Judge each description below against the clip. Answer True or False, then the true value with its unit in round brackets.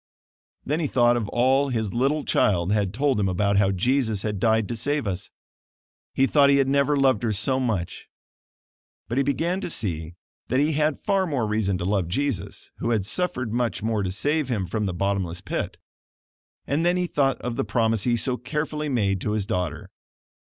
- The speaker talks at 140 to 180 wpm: False (200 wpm)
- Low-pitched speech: True (120 Hz)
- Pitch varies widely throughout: True (5.7 semitones)